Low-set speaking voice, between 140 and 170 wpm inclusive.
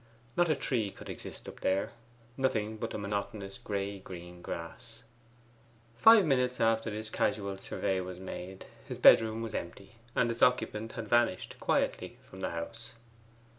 Yes: low, 110 Hz; average, 155 wpm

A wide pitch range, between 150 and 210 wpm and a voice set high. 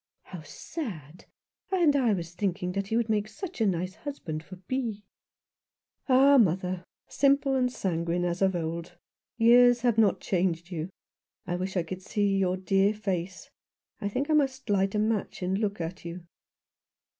No: average, 4.7 semitones; average, 170 wpm; high, 195 Hz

